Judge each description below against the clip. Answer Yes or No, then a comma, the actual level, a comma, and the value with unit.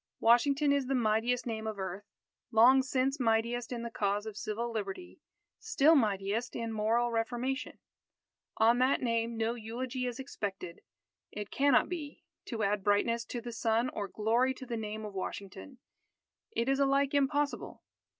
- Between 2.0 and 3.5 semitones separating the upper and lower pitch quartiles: Yes, average, 3.2 semitones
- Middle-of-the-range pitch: No, high, 235 Hz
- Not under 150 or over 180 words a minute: Yes, average, 155 wpm